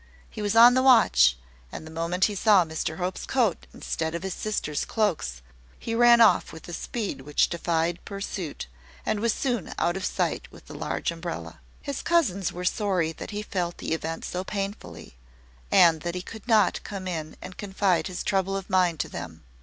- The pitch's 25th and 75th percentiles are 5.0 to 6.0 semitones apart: No, average, 4.2 semitones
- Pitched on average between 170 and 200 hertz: Yes, medium, 185 Hz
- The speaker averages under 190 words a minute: No, average, 195 wpm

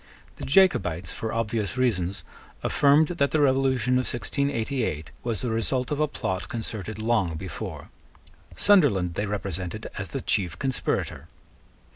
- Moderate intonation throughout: No, wide, 5.8 semitones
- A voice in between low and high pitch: No, low, 115 Hz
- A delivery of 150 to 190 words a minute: No, slow, 135 wpm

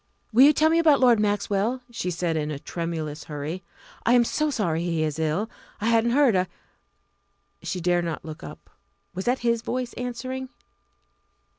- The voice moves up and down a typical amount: No, wide, 6.9 semitones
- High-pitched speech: Yes, high, 205 Hz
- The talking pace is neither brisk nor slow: Yes, average, 180 wpm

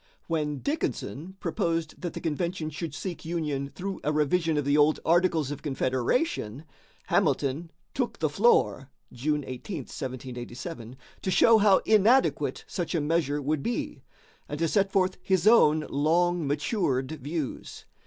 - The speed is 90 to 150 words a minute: Yes, average, 145 wpm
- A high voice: No, medium, 155 Hz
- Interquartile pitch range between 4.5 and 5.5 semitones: No, average, 4.0 semitones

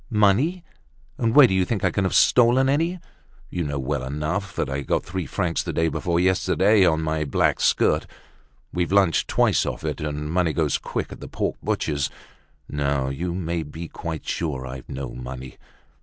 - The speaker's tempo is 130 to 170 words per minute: No, average, 185 wpm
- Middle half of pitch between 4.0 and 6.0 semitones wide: Yes, average, 5.1 semitones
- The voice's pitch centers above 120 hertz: No, very low, 85 Hz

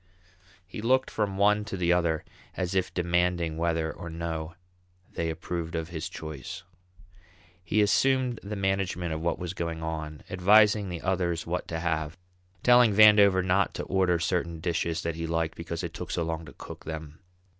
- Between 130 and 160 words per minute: No, average, 175 wpm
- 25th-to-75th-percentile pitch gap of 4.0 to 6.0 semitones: No, average, 2.8 semitones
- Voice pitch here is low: Yes, very low, 85 Hz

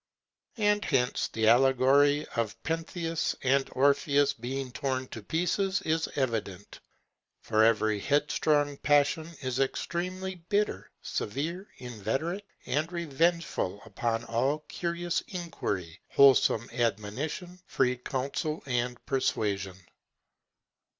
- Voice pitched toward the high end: No, medium, 140 Hz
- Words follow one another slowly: Yes, slow, 100 wpm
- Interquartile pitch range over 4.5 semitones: Yes, wide, 5.6 semitones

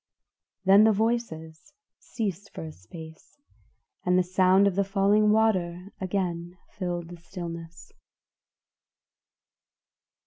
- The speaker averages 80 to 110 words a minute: Yes, slow, 105 wpm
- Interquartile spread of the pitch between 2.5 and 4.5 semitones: Yes, average, 2.8 semitones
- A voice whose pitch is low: No, medium, 185 Hz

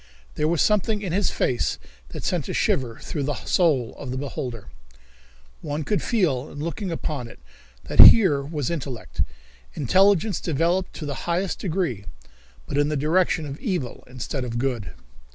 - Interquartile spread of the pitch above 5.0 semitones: Yes, wide, 5.5 semitones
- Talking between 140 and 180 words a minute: Yes, average, 165 wpm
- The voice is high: No, medium, 150 Hz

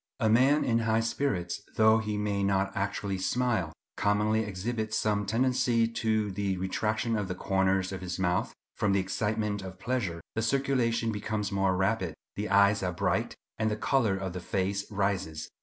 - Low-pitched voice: Yes, low, 105 Hz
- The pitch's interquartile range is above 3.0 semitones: No, average, 2.7 semitones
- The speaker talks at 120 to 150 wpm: No, average, 175 wpm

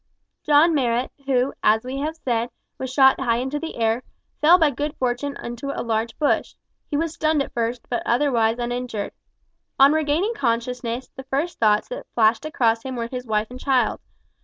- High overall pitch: Yes, very high, 255 Hz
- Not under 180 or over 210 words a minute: Yes, average, 185 wpm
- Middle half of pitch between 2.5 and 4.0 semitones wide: Yes, average, 3.7 semitones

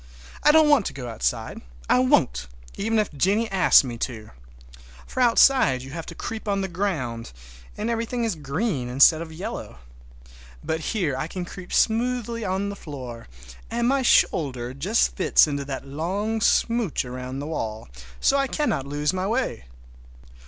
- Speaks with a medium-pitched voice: Yes, medium, 175 Hz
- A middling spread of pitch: No, wide, 9.0 semitones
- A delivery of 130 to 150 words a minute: No, average, 165 wpm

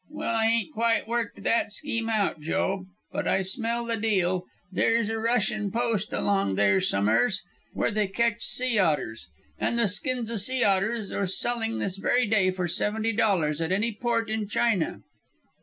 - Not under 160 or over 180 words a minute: Yes, average, 175 wpm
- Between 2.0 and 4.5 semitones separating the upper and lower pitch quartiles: Yes, average, 3.4 semitones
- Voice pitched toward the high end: Yes, high, 215 Hz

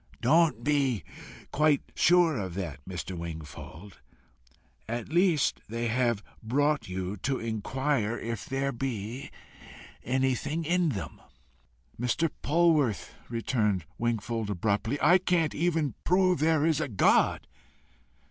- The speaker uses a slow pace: Yes, slow, 115 wpm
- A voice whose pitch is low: Yes, low, 130 Hz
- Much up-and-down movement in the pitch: Yes, wide, 6.4 semitones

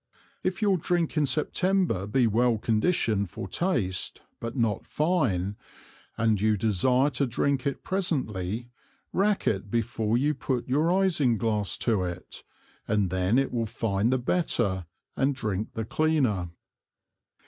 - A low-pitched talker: Yes, low, 120 Hz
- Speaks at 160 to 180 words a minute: No, average, 140 wpm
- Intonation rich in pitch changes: Yes, wide, 6.1 semitones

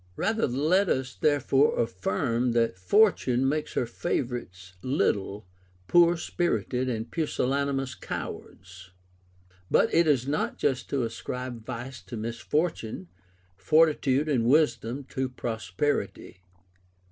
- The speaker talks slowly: Yes, slow, 110 wpm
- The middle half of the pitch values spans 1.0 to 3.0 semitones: No, average, 4.3 semitones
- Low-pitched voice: Yes, low, 125 Hz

